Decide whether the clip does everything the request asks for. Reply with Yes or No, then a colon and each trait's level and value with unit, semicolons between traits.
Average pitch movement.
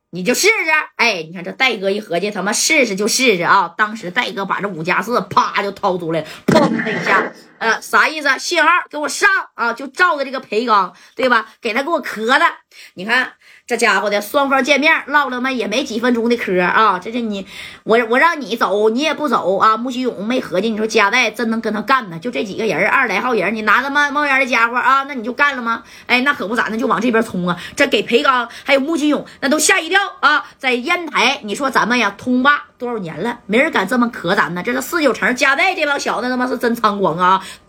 Yes: average, 4.9 semitones